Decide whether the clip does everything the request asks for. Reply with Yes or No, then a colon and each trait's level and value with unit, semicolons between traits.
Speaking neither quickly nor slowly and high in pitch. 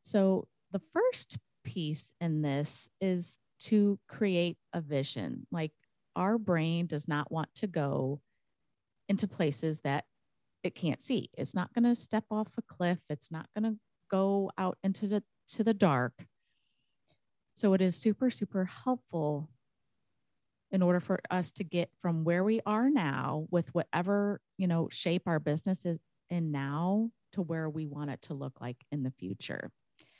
No: average, 165 wpm; medium, 175 Hz